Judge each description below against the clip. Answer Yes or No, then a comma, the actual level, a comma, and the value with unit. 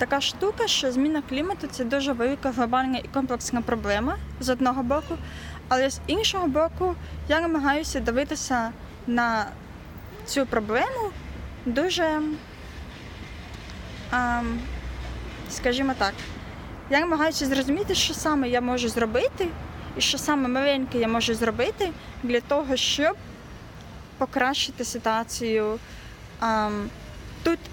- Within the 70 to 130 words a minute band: Yes, slow, 105 wpm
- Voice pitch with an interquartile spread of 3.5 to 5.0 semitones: Yes, average, 4.1 semitones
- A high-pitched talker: Yes, very high, 265 Hz